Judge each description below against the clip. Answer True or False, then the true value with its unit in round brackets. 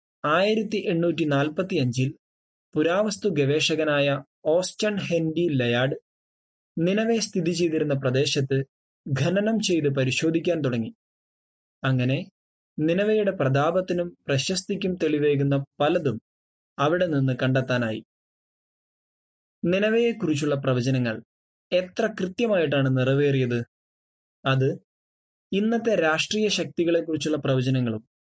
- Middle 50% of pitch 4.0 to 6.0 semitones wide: True (5.6 semitones)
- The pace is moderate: True (75 wpm)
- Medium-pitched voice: True (155 Hz)